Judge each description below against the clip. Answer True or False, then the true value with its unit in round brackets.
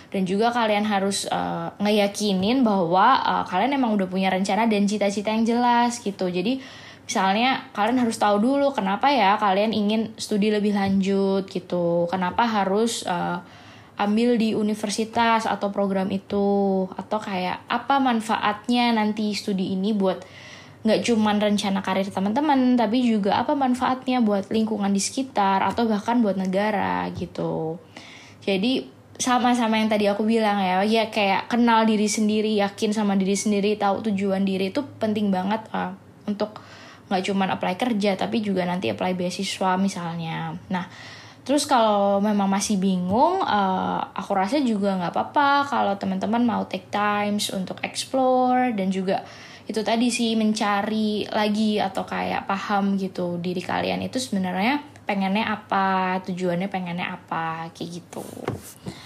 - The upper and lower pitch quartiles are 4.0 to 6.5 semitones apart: False (2.7 semitones)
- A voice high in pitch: True (205 Hz)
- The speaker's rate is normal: False (145 wpm)